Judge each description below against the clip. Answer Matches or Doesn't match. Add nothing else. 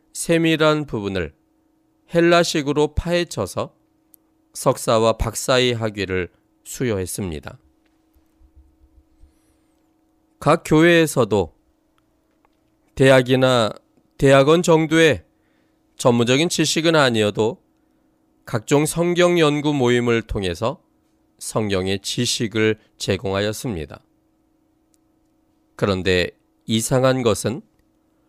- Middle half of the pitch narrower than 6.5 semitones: Doesn't match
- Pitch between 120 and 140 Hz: Matches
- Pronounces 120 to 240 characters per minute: Matches